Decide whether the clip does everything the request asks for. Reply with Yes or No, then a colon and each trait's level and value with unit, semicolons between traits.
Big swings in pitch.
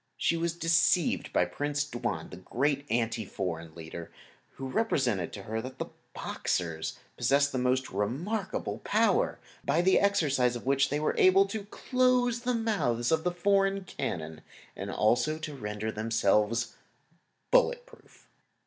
Yes: wide, 9.0 semitones